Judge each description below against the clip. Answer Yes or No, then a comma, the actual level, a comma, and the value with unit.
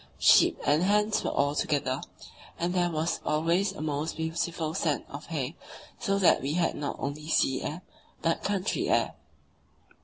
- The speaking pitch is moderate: Yes, medium, 160 Hz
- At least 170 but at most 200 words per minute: No, average, 160 wpm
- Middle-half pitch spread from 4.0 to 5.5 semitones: No, average, 3.1 semitones